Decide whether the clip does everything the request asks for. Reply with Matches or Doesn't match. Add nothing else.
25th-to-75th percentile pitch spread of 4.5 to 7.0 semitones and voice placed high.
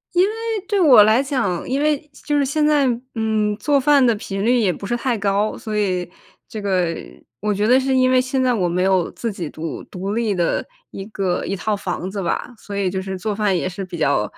Matches